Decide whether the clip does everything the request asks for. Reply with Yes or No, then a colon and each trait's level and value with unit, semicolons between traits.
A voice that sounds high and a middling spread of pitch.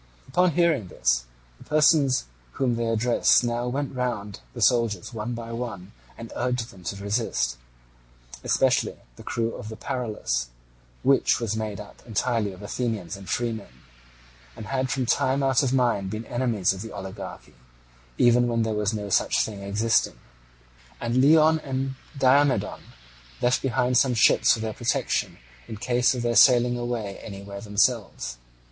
No: low, 115 Hz; average, 3.5 semitones